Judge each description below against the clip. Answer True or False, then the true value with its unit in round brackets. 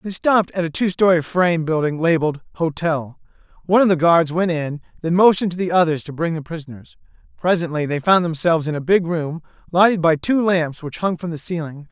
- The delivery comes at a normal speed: False (210 wpm)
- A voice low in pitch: False (165 Hz)